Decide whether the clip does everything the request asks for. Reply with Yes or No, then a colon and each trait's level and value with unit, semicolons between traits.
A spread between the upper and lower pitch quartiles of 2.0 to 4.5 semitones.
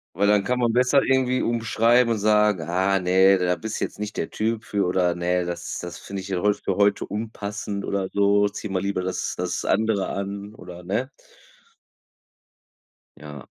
Yes: average, 2.7 semitones